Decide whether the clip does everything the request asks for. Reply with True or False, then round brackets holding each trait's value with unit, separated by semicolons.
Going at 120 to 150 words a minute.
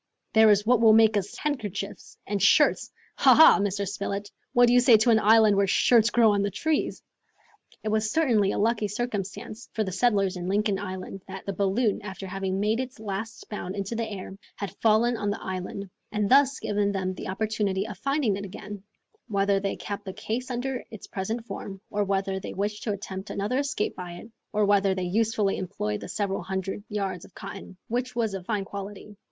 False (205 wpm)